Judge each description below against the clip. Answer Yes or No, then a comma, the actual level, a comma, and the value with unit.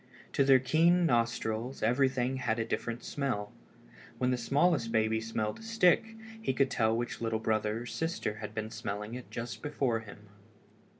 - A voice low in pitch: Yes, low, 120 Hz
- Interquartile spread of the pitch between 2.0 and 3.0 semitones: No, average, 3.6 semitones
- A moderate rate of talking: Yes, average, 170 wpm